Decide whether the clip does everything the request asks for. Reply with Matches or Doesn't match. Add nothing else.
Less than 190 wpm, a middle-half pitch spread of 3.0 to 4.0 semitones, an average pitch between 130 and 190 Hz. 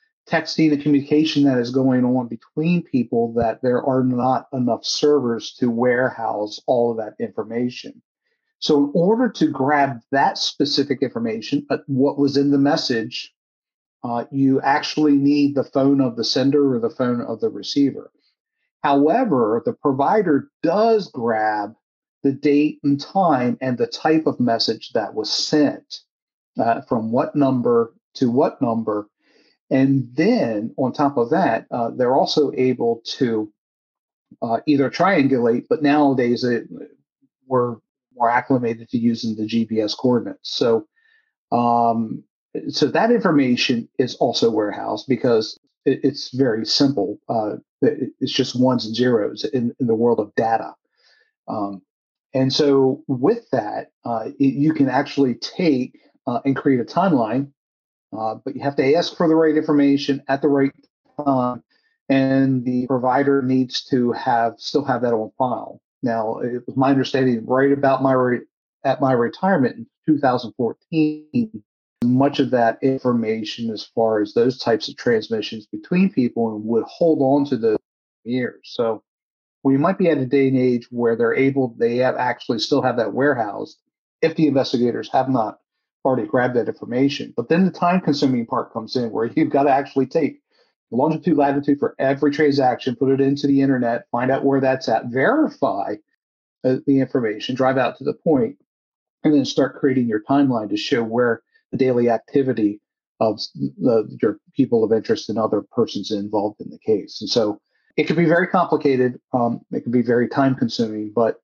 Matches